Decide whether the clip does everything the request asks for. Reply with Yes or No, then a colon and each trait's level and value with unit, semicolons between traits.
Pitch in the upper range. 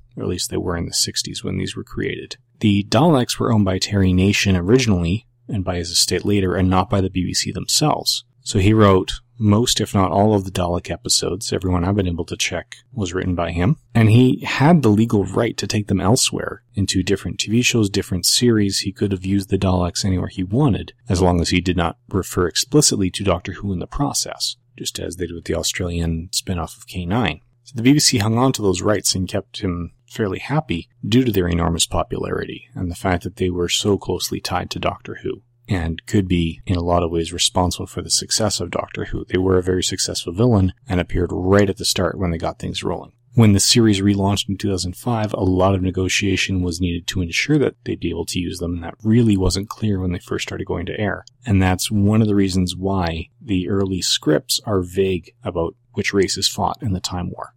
No: very low, 95 Hz